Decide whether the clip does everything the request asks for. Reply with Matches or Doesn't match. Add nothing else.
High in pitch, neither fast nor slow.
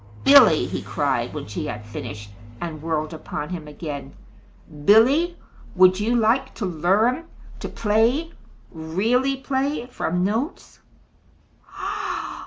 Doesn't match